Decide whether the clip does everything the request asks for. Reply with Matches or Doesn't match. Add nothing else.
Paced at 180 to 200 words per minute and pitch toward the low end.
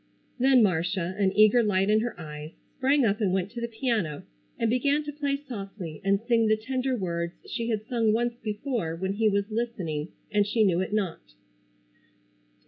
Doesn't match